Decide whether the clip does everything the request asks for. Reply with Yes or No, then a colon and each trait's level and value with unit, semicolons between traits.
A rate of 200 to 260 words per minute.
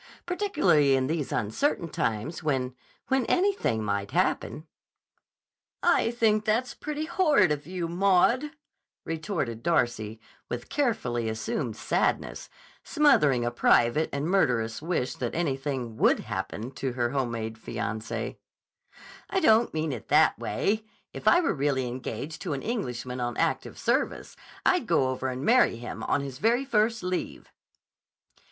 No: average, 140 wpm